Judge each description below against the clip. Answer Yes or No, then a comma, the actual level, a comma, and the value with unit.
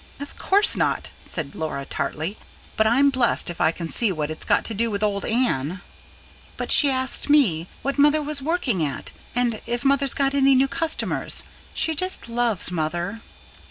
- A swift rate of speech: No, average, 180 wpm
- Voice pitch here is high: Yes, high, 235 Hz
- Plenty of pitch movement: Yes, wide, 8.1 semitones